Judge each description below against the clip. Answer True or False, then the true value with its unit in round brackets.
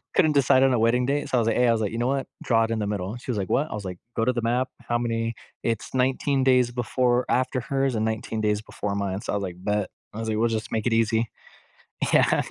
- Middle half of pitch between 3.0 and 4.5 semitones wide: False (2.6 semitones)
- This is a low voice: True (115 Hz)